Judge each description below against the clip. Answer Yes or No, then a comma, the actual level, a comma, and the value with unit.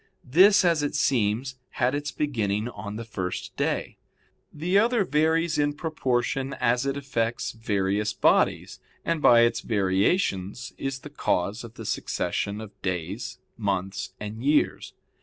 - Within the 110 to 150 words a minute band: Yes, average, 140 wpm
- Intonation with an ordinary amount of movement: No, wide, 6.0 semitones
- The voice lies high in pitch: No, low, 120 Hz